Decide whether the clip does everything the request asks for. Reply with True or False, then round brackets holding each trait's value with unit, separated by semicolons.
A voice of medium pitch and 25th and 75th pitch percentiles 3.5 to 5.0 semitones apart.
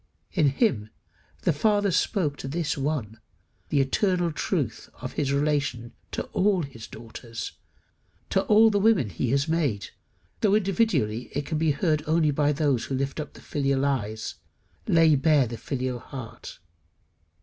True (145 Hz; 4.6 semitones)